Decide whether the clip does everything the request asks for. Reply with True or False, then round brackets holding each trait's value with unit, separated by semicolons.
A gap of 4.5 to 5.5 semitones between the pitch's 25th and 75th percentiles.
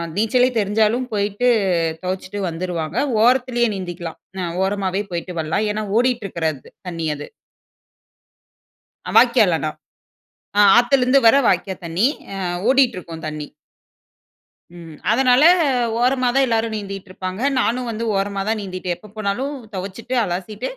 True (5.0 semitones)